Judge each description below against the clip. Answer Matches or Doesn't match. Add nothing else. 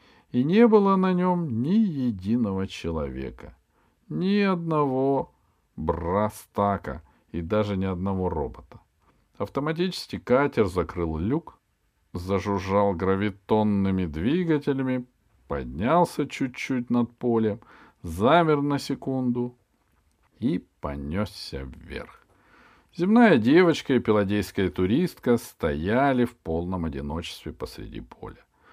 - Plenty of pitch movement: Matches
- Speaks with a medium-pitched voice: Doesn't match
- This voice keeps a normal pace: Doesn't match